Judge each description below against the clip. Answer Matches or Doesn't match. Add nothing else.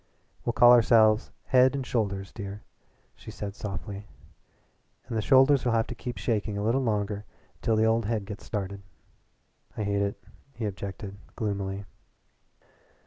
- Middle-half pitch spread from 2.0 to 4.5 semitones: Matches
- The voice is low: Matches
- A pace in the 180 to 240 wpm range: Doesn't match